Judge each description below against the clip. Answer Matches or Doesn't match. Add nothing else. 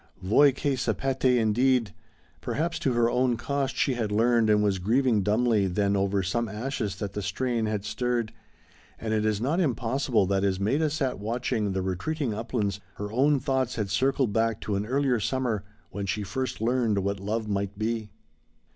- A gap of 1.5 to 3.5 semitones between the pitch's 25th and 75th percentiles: Doesn't match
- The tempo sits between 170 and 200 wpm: Matches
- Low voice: Matches